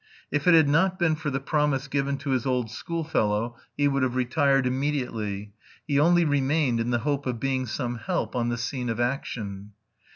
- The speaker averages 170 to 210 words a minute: Yes, average, 195 wpm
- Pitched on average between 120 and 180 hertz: Yes, low, 135 Hz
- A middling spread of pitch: Yes, average, 3.4 semitones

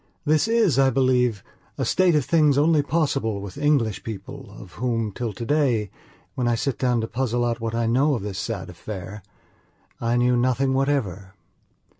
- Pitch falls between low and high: No, low, 120 Hz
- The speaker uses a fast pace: No, average, 175 wpm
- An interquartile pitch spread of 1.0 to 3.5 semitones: No, average, 4.2 semitones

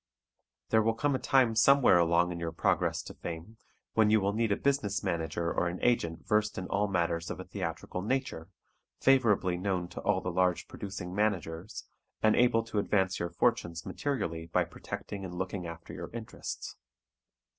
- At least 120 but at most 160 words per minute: No, average, 175 wpm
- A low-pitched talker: Yes, very low, 95 Hz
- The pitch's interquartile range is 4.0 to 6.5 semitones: Yes, average, 4.5 semitones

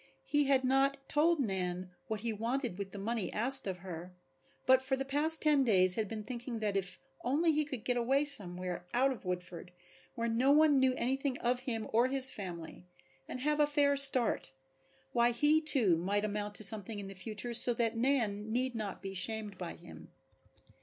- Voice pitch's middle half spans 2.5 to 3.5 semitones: No, average, 5.2 semitones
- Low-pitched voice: No, high, 235 Hz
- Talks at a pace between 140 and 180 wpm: No, average, 195 wpm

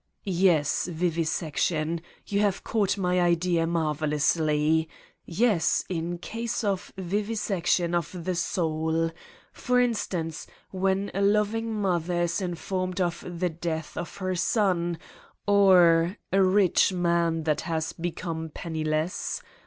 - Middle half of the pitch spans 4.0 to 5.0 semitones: No, average, 2.9 semitones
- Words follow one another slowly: Yes, slow, 120 wpm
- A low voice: No, medium, 175 Hz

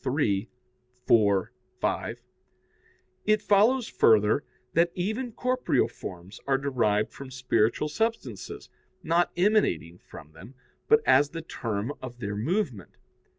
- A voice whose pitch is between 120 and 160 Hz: Yes, low, 135 Hz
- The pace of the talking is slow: Yes, slow, 115 wpm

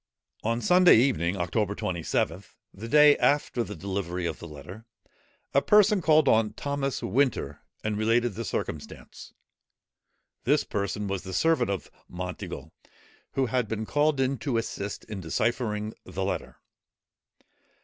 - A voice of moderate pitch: No, low, 110 Hz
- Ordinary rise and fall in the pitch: No, wide, 6.1 semitones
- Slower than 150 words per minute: Yes, average, 140 wpm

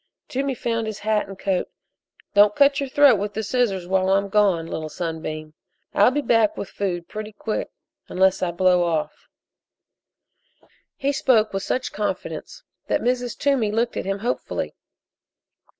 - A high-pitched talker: Yes, high, 210 Hz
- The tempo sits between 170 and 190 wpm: No, average, 160 wpm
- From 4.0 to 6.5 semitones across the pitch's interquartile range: Yes, average, 4.4 semitones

